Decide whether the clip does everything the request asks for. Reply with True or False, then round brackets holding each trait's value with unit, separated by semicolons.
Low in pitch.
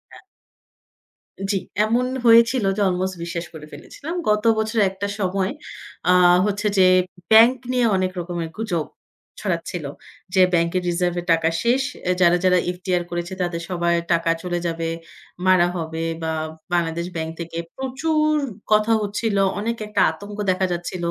False (185 Hz)